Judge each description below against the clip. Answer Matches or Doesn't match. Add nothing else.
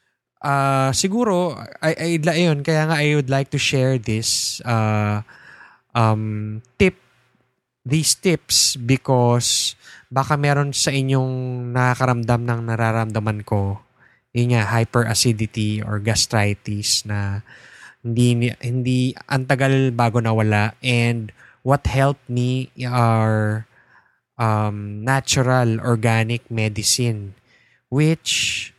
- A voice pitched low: Matches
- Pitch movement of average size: Matches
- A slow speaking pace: Matches